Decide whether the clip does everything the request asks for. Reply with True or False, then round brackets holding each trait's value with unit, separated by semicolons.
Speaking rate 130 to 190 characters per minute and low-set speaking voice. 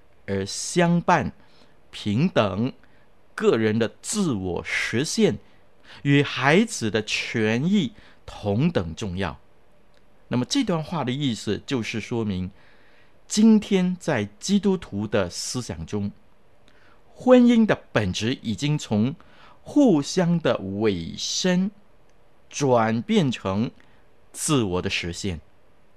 True (150 characters per minute; 120 Hz)